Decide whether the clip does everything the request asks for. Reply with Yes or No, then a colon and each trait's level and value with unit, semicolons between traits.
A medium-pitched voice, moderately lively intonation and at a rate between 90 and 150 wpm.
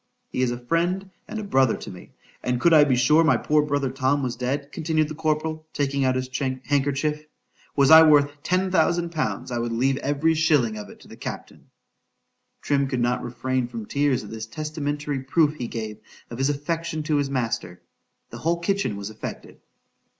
No: medium, 145 Hz; average, 3.6 semitones; average, 180 wpm